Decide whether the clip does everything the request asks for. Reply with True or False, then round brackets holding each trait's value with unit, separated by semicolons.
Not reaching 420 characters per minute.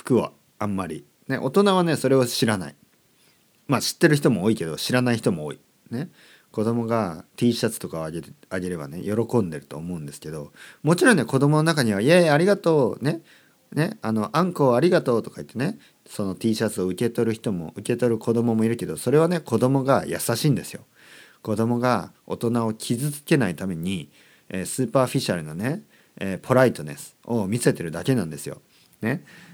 True (345 characters per minute)